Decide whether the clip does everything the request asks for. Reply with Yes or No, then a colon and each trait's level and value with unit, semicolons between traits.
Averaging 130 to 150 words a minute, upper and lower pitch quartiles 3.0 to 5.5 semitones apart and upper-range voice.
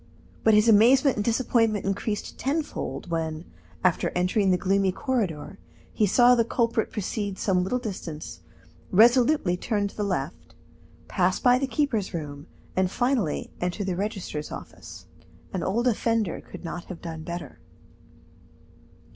Yes: average, 140 wpm; average, 4.6 semitones; high, 200 Hz